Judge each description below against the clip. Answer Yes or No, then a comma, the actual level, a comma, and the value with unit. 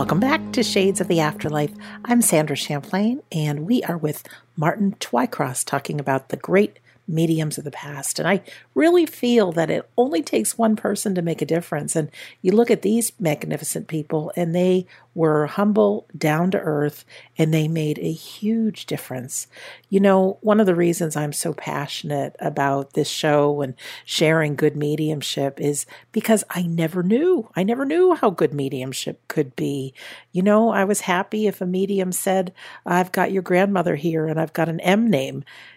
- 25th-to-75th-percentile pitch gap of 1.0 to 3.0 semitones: No, average, 5.2 semitones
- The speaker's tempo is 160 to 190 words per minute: Yes, average, 180 wpm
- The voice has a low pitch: No, medium, 175 Hz